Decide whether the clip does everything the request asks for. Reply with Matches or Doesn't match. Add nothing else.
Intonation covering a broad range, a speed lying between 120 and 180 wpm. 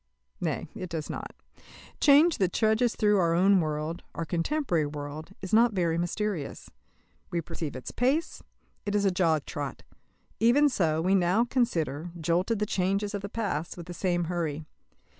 Doesn't match